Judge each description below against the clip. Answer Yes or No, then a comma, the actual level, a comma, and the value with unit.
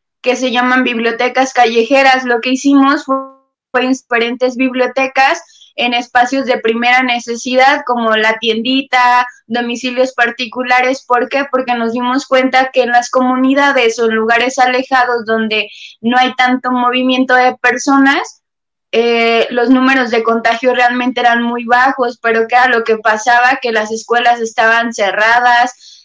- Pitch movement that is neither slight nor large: No, narrow, 1.5 semitones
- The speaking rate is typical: Yes, average, 145 wpm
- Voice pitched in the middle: No, high, 245 Hz